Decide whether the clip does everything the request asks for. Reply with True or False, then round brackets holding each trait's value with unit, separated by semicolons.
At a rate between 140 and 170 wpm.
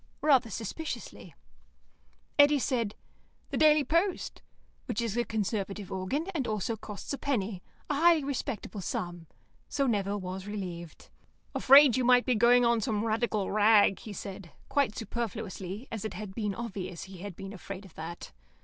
True (160 wpm)